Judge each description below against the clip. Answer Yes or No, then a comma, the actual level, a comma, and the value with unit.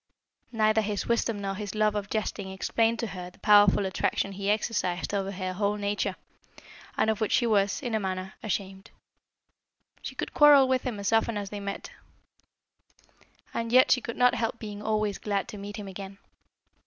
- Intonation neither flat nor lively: No, narrow, 2.2 semitones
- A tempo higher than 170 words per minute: Yes, average, 185 wpm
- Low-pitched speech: No, high, 205 Hz